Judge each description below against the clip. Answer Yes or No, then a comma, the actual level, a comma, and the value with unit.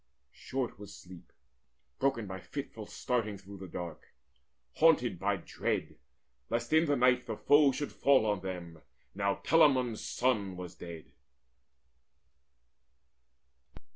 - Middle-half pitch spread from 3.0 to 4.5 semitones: No, wide, 5.6 semitones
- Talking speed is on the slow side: Yes, slow, 120 wpm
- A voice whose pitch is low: Yes, low, 110 Hz